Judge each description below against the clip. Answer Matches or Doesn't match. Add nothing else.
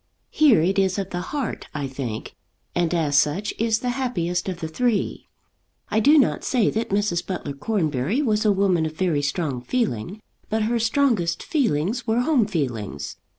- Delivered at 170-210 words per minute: Matches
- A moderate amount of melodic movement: Doesn't match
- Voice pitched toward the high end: Matches